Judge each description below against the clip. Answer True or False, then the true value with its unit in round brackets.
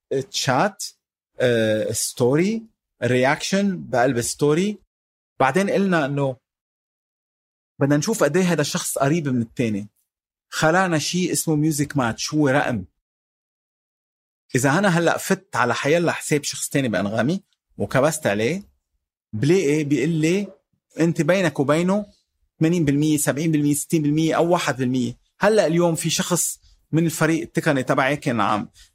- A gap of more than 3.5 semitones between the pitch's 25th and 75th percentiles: True (5.0 semitones)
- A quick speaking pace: False (120 wpm)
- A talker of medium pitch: True (150 Hz)